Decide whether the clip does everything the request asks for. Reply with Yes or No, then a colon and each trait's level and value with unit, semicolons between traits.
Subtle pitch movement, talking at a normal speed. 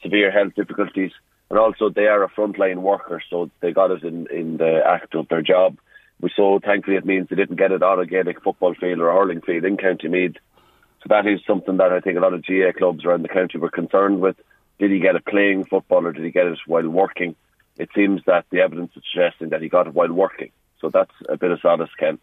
No: narrow, 2.2 semitones; fast, 255 wpm